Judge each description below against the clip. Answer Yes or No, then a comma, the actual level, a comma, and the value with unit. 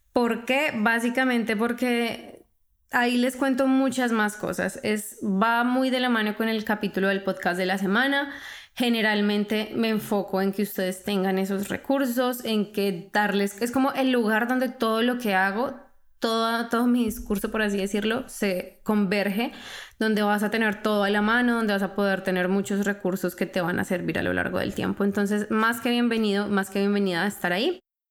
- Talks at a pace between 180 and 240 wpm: Yes, fast, 190 wpm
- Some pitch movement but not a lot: Yes, average, 3.2 semitones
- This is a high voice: Yes, high, 215 Hz